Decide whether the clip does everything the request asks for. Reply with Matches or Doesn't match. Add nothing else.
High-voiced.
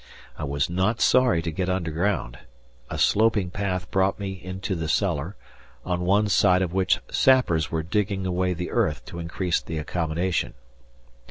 Doesn't match